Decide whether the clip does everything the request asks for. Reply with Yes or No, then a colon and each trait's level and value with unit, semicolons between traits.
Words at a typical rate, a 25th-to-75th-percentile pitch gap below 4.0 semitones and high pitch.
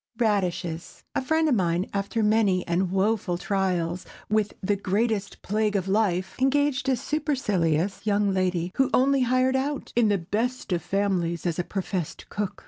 No: average, 160 wpm; average, 4.7 semitones; high, 200 Hz